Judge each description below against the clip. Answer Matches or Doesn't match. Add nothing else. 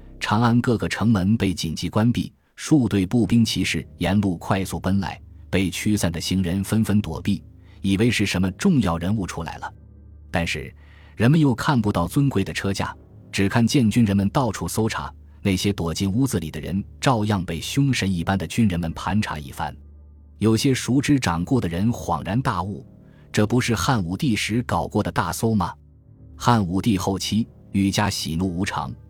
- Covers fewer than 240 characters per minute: Doesn't match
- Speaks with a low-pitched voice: Matches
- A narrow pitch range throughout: Doesn't match